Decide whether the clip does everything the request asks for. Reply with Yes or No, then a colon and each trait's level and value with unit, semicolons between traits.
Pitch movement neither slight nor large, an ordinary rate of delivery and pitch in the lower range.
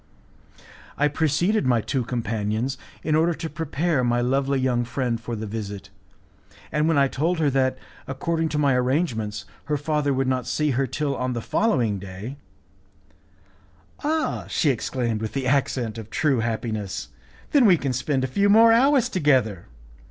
Yes: average, 4.6 semitones; average, 165 wpm; low, 130 Hz